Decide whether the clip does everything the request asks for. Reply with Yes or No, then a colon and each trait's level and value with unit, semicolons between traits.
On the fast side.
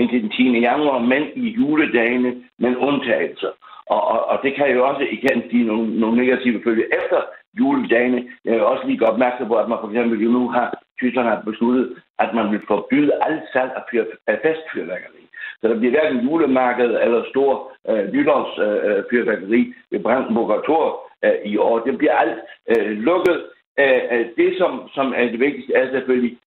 No: average, 180 wpm